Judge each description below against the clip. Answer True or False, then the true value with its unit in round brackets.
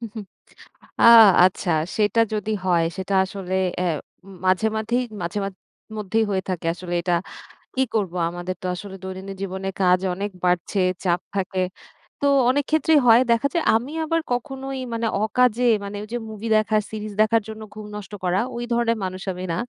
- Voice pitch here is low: False (210 Hz)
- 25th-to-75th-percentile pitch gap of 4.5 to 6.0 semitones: False (3.7 semitones)